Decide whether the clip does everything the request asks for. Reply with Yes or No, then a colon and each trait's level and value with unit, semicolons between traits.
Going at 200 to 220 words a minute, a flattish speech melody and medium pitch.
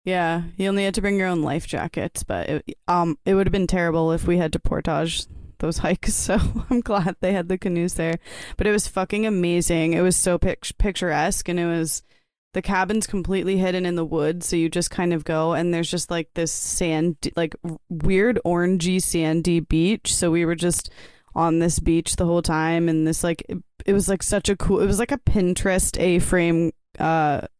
Yes: fast, 205 wpm; narrow, 2.3 semitones; medium, 175 Hz